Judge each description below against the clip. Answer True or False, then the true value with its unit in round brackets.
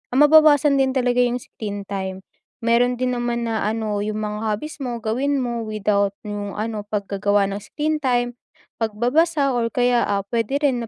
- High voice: True (235 Hz)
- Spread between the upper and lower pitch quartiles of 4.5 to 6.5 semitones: False (3.5 semitones)